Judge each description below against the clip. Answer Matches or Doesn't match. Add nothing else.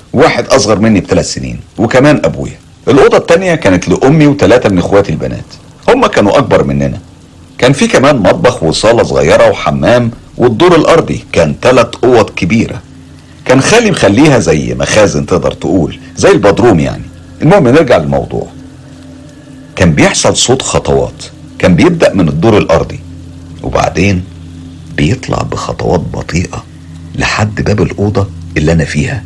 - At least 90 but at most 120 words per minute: Doesn't match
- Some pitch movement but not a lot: Matches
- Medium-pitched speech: Doesn't match